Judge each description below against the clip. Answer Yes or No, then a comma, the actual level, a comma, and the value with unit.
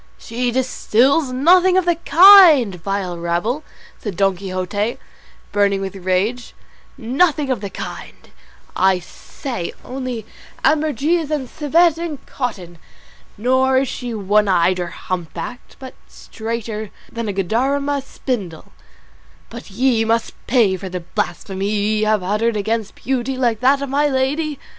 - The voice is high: Yes, high, 230 Hz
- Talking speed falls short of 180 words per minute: Yes, slow, 135 wpm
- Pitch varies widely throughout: Yes, wide, 5.7 semitones